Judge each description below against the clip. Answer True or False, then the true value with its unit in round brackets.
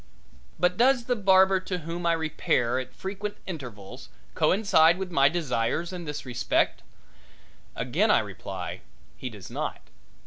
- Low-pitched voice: False (170 Hz)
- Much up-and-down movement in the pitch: True (5.7 semitones)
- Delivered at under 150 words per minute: True (140 wpm)